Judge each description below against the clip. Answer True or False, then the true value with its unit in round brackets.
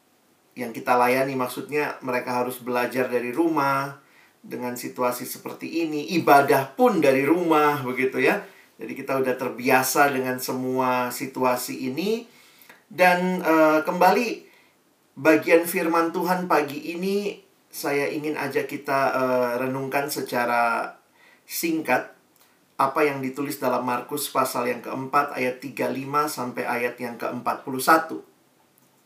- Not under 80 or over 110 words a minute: False (120 wpm)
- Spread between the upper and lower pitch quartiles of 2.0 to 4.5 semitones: True (3.6 semitones)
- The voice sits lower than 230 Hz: True (135 Hz)